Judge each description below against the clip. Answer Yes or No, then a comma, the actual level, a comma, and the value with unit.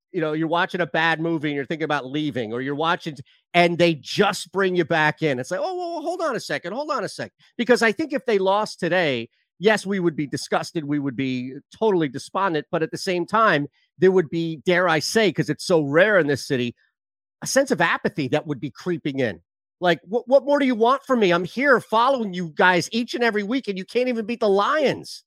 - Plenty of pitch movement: Yes, wide, 6.2 semitones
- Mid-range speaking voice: Yes, medium, 175 Hz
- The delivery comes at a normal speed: No, fast, 250 wpm